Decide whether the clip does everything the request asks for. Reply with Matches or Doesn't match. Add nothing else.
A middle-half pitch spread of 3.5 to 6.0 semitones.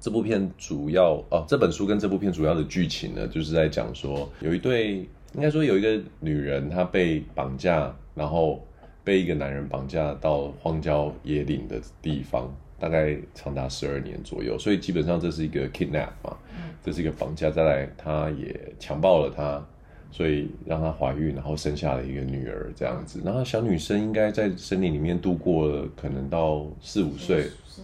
Matches